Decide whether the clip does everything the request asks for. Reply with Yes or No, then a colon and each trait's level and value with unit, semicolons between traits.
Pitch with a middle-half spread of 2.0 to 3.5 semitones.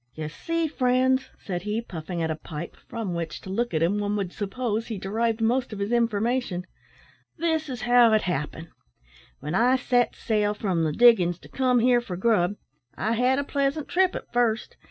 No: average, 5.3 semitones